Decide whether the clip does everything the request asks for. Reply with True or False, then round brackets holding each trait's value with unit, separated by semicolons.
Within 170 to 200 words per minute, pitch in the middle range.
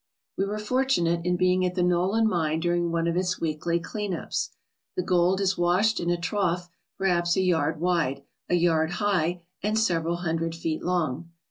True (185 wpm; 175 Hz)